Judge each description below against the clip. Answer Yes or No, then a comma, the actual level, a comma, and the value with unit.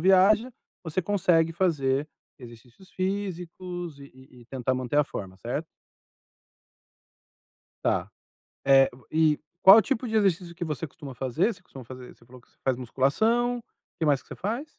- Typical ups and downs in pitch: No, wide, 6.4 semitones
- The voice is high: No, medium, 160 Hz